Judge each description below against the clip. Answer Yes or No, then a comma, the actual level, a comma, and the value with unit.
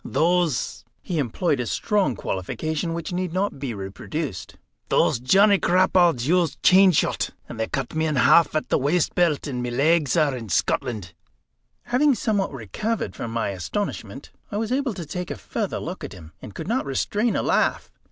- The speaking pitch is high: No, medium, 155 Hz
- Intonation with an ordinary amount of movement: No, wide, 7.1 semitones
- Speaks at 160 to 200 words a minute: Yes, average, 180 wpm